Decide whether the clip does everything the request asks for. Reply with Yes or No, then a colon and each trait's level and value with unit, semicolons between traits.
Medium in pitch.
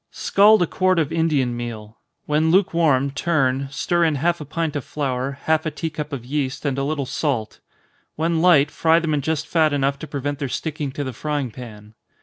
Yes: medium, 145 Hz